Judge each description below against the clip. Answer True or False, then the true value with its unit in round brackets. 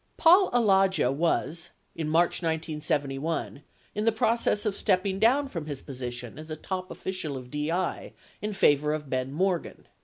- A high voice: False (165 Hz)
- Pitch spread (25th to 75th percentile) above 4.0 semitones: True (4.8 semitones)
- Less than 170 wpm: True (155 wpm)